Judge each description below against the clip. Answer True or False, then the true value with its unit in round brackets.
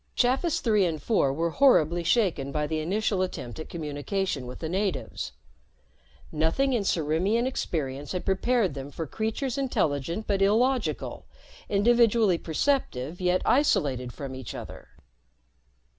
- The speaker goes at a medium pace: False (130 wpm)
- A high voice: False (180 Hz)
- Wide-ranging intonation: True (7.1 semitones)